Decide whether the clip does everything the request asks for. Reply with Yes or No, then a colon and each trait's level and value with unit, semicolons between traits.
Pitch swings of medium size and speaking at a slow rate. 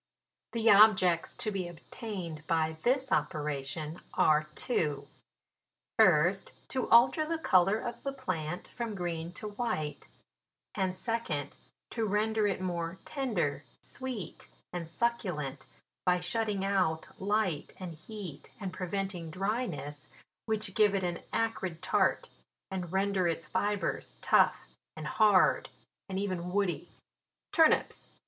Yes: average, 4.6 semitones; slow, 130 wpm